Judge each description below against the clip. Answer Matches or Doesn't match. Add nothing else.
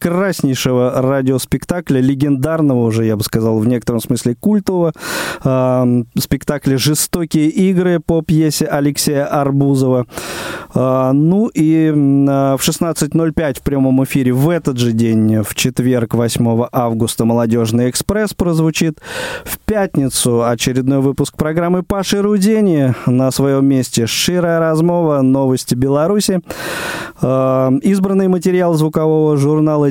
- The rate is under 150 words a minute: Matches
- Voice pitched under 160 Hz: Matches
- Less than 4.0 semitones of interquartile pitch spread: Doesn't match